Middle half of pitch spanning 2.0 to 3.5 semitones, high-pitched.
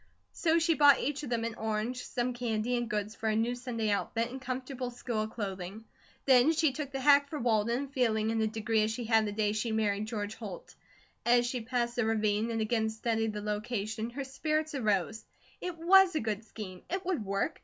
Yes: average, 3.1 semitones; high, 230 Hz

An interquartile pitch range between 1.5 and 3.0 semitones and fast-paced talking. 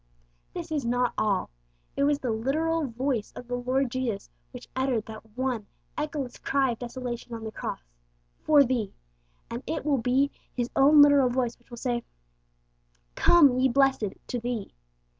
No: average, 2.7 semitones; average, 165 wpm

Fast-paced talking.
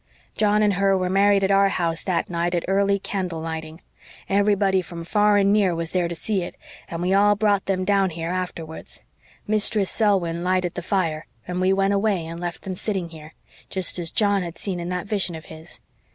Yes: fast, 210 wpm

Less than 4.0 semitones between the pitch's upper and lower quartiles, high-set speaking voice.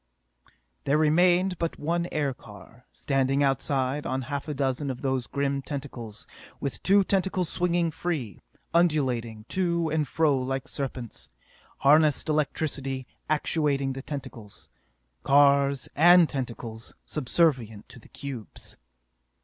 No: average, 3.3 semitones; medium, 140 Hz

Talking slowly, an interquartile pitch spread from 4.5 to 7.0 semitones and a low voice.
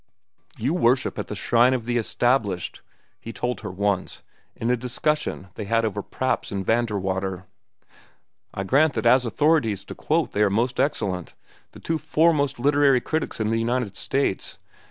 No: average, 160 wpm; average, 4.9 semitones; low, 120 Hz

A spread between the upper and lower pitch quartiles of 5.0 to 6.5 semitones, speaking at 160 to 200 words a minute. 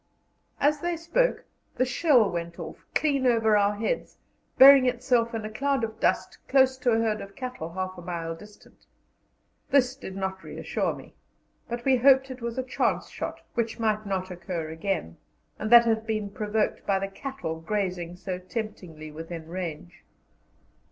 Yes: wide, 5.6 semitones; average, 170 wpm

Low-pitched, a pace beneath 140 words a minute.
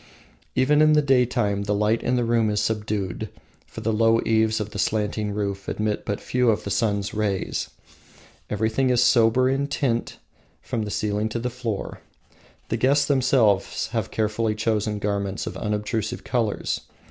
No: low, 110 Hz; average, 165 wpm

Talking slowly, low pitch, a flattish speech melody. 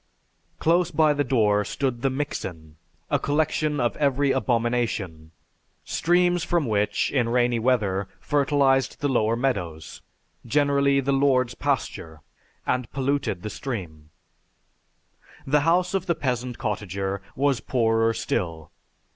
No: slow, 120 wpm; low, 125 Hz; average, 5.2 semitones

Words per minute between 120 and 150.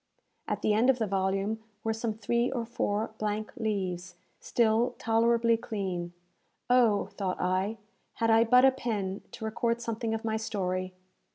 No: average, 160 wpm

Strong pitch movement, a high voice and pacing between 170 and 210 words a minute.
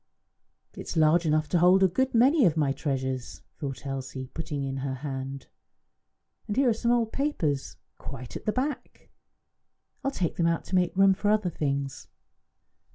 No: wide, 7.4 semitones; medium, 165 Hz; average, 180 wpm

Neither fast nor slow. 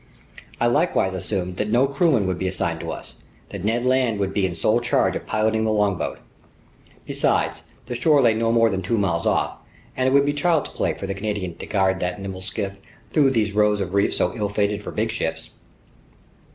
No: fast, 210 wpm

